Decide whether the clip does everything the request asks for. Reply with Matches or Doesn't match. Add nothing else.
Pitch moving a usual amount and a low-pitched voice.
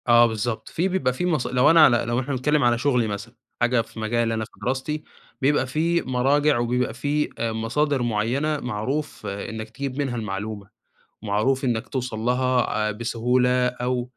Matches